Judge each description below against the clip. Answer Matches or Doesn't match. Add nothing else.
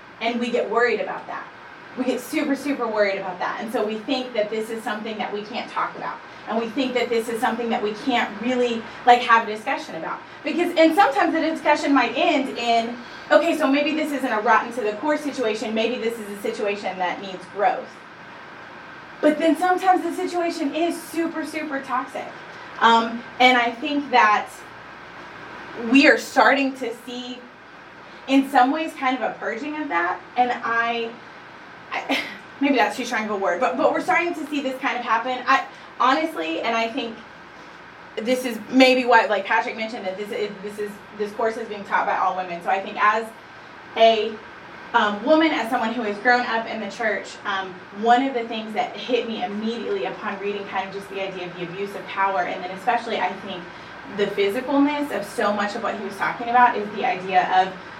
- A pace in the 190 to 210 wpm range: Matches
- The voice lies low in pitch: Doesn't match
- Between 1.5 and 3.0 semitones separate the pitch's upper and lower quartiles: Doesn't match